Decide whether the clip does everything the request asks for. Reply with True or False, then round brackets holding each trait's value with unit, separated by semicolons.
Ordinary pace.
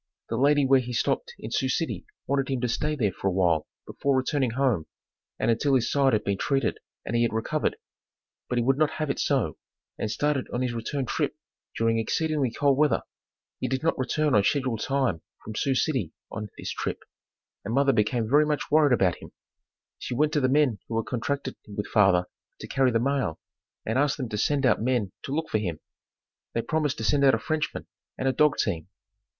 False (210 wpm)